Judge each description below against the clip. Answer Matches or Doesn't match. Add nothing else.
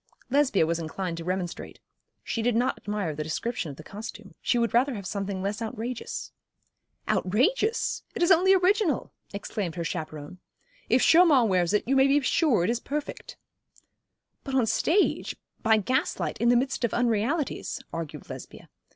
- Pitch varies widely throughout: Matches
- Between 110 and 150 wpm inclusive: Doesn't match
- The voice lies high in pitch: Matches